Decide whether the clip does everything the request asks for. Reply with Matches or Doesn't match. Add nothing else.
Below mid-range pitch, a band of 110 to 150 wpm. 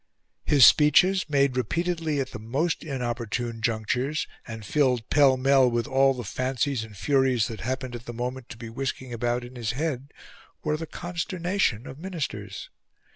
Doesn't match